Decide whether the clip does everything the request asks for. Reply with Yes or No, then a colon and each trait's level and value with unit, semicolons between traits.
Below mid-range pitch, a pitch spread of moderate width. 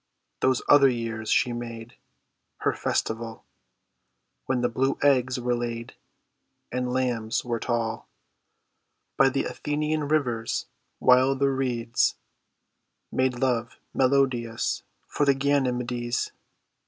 No: low, 125 Hz; narrow, 2.2 semitones